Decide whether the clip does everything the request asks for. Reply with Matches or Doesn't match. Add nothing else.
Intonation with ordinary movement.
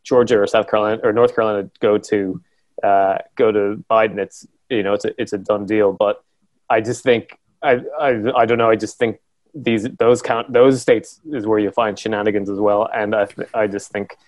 Doesn't match